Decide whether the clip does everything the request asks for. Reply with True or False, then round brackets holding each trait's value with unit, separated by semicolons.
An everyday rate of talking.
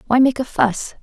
False (235 wpm)